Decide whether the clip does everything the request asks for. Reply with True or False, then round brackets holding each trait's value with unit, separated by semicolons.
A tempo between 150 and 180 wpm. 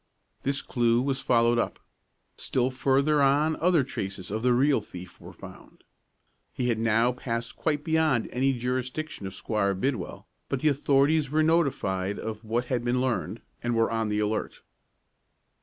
True (160 wpm)